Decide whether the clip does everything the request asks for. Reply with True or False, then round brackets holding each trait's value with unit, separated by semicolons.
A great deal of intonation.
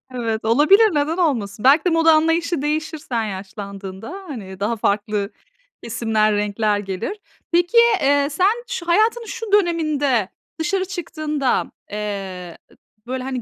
True (8.2 semitones)